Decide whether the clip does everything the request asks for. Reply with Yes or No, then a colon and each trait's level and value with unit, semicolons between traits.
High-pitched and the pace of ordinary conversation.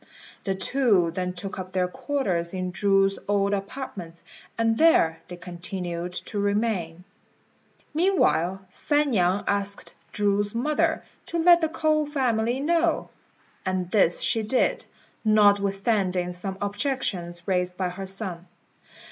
No: high, 200 Hz; slow, 125 wpm